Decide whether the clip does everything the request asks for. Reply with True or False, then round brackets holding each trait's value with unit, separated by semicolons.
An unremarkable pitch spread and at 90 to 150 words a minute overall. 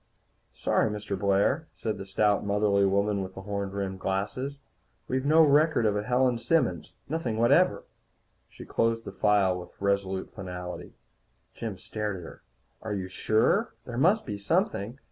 False (4.1 semitones; 160 wpm)